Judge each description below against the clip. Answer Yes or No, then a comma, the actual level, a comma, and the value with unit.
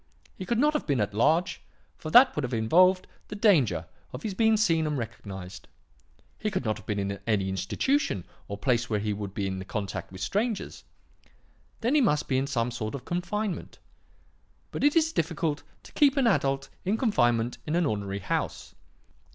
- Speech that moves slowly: No, average, 190 wpm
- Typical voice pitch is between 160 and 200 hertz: No, medium, 140 Hz